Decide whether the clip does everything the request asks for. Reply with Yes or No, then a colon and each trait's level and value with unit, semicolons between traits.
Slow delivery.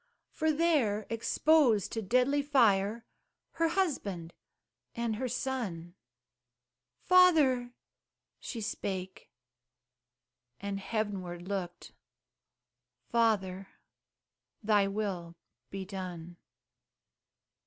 Yes: slow, 75 wpm